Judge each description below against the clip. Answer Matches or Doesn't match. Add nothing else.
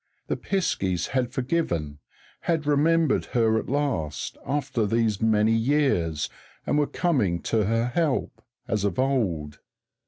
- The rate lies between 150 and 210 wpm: Doesn't match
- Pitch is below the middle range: Matches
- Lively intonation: Matches